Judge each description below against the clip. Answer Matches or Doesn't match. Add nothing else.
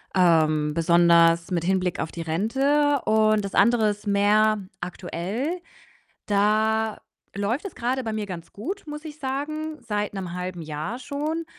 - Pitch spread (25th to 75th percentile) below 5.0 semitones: Doesn't match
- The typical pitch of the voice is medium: Doesn't match